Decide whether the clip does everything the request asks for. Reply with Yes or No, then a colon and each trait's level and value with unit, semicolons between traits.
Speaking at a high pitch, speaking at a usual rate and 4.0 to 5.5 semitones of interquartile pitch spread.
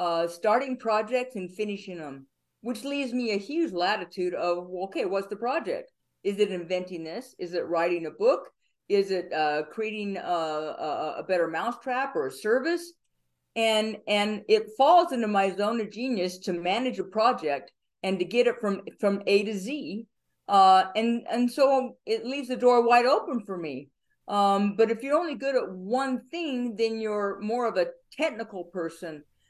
Yes: high, 215 Hz; average, 180 wpm; average, 5.2 semitones